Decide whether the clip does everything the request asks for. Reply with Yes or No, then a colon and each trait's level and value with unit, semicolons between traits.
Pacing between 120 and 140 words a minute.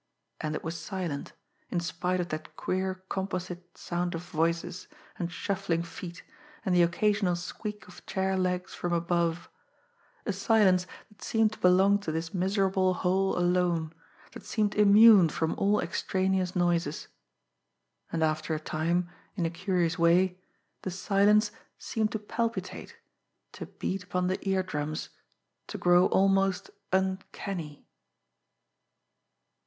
Yes: slow, 135 wpm